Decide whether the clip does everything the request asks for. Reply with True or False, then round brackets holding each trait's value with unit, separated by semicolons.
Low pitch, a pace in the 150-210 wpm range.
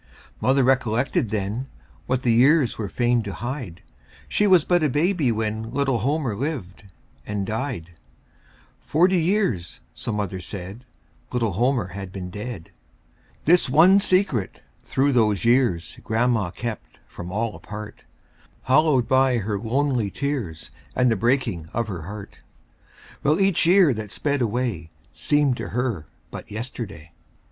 False (120 Hz; 140 wpm)